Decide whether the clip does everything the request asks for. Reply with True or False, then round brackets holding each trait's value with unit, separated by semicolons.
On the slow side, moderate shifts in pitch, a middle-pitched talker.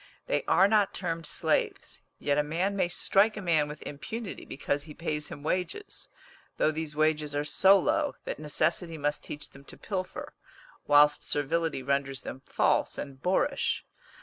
False (165 wpm; 4.4 semitones; 155 Hz)